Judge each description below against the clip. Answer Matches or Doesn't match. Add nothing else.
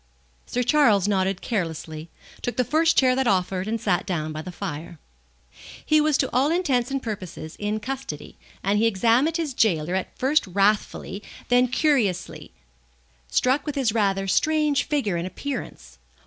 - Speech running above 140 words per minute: Matches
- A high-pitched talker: Matches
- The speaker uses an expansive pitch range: Matches